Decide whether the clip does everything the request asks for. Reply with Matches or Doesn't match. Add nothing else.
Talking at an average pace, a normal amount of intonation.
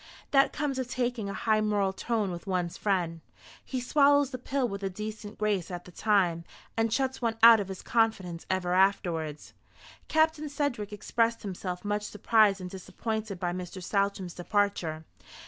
Matches